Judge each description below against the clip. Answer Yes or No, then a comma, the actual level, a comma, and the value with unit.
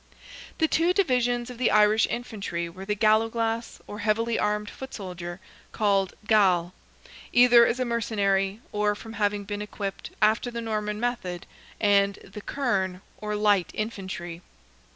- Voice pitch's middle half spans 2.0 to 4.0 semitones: Yes, average, 2.8 semitones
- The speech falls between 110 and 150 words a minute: Yes, average, 145 wpm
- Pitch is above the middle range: Yes, high, 210 Hz